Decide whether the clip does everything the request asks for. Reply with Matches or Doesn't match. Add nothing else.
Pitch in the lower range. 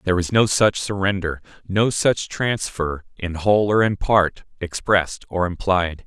Matches